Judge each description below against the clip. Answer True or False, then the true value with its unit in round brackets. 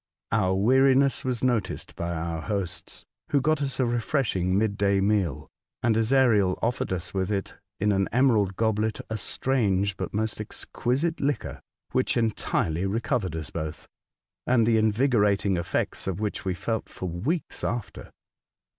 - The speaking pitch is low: True (110 Hz)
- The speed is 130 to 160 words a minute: True (155 wpm)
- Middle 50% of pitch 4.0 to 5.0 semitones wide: True (4.5 semitones)